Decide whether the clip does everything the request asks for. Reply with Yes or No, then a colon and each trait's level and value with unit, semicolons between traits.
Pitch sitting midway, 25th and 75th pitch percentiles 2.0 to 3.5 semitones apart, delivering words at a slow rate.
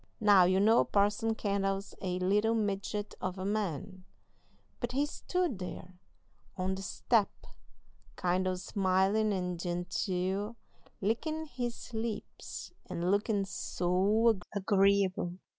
No: high, 200 Hz; average, 2.8 semitones; slow, 115 wpm